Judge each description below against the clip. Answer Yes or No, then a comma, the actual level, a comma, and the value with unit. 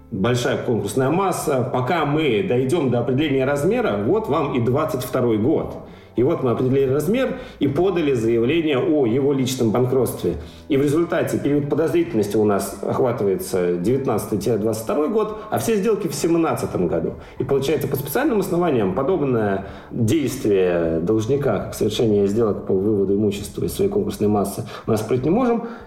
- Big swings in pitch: Yes, wide, 8.1 semitones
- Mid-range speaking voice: No, low, 130 Hz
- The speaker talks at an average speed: Yes, average, 150 wpm